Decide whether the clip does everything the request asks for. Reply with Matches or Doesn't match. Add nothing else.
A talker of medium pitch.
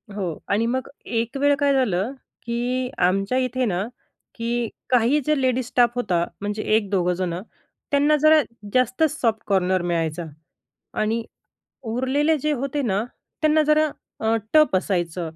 Doesn't match